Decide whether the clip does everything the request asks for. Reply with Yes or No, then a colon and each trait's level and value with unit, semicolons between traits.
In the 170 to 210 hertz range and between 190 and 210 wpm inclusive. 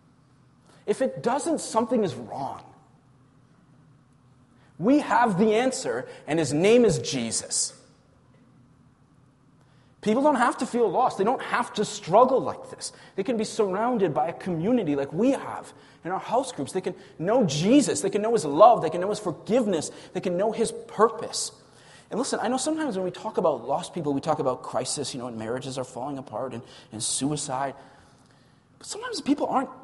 No: medium, 185 Hz; average, 180 wpm